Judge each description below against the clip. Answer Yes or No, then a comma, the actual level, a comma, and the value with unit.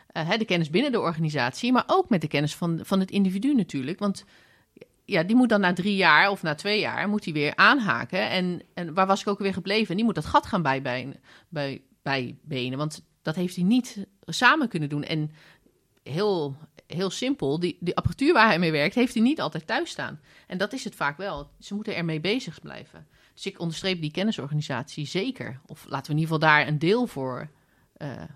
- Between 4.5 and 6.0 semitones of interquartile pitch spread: Yes, wide, 5.4 semitones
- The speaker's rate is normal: No, fast, 215 wpm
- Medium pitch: Yes, medium, 175 Hz